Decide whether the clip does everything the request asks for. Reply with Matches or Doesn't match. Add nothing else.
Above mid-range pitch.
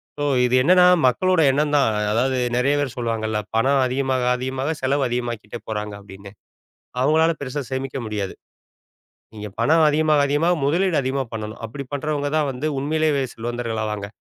Doesn't match